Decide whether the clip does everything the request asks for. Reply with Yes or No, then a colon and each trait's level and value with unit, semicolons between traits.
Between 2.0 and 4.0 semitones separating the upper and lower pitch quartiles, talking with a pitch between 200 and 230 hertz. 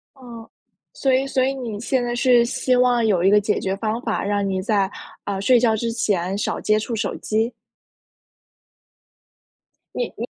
Yes: average, 3.3 semitones; high, 225 Hz